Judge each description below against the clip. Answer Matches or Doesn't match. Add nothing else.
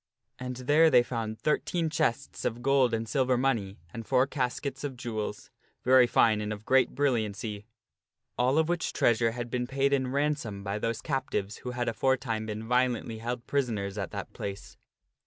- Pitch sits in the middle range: Doesn't match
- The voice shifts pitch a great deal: Doesn't match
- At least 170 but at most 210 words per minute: Matches